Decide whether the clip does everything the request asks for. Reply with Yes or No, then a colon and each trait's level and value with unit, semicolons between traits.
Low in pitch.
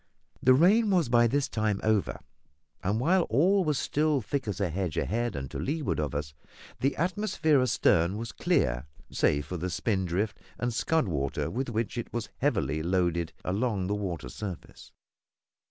Yes: low, 110 Hz